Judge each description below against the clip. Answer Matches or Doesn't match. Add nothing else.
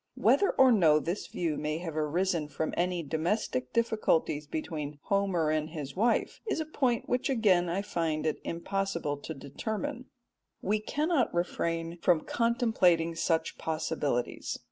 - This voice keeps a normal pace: Matches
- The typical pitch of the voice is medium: Matches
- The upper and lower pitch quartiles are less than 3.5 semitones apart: Doesn't match